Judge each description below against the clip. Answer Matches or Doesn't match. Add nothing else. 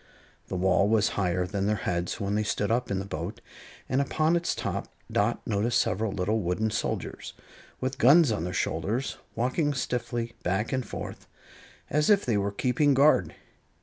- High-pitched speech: Doesn't match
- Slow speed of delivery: Doesn't match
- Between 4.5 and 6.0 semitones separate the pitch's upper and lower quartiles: Matches